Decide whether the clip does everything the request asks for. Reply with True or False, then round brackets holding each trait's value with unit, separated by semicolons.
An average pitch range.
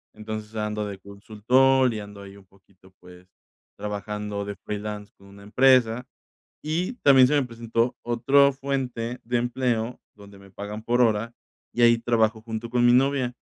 True (3.2 semitones)